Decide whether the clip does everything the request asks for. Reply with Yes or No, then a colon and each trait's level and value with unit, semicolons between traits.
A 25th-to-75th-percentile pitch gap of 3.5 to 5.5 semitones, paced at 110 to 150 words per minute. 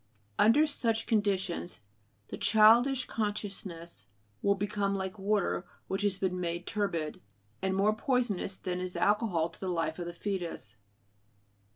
No: average, 3.1 semitones; average, 140 wpm